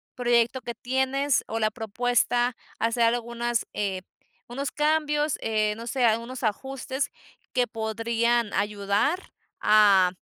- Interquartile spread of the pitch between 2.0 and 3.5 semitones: Yes, average, 2.9 semitones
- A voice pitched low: No, high, 235 Hz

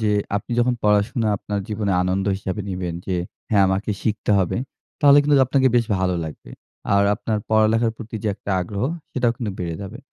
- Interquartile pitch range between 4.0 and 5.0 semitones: No, average, 3.2 semitones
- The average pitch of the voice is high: No, low, 105 Hz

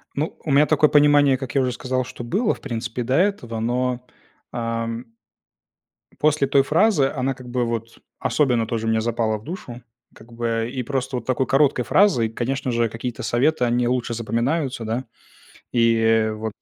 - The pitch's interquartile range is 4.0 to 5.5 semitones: No, average, 3.0 semitones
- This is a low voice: Yes, low, 125 Hz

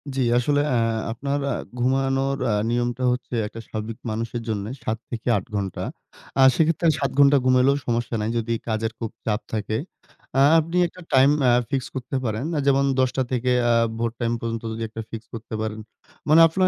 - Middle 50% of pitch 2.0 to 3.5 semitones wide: Yes, average, 3.2 semitones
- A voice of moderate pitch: No, low, 120 Hz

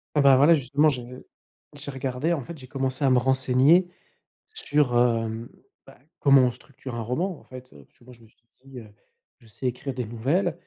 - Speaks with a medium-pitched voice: No, low, 130 Hz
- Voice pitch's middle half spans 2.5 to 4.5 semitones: Yes, average, 2.8 semitones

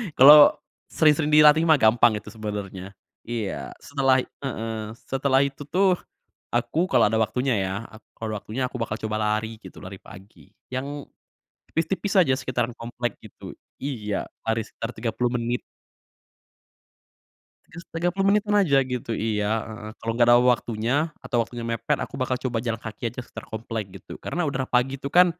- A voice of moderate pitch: No, low, 120 Hz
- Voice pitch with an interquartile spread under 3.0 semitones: No, average, 4.2 semitones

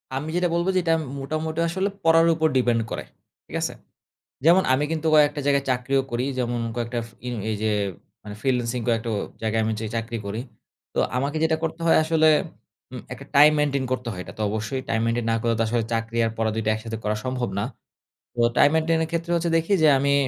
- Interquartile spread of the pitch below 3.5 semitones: No, wide, 5.6 semitones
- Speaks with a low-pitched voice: Yes, low, 130 Hz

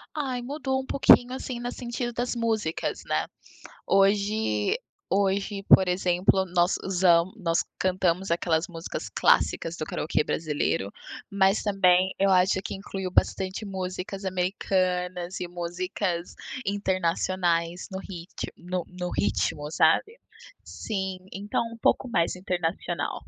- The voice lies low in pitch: No, medium, 185 Hz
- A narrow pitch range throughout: Yes, narrow, 2.3 semitones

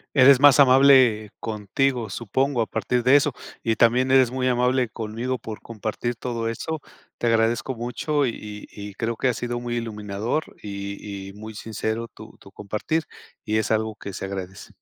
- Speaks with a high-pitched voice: No, low, 115 Hz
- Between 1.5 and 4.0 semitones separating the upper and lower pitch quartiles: Yes, average, 3.1 semitones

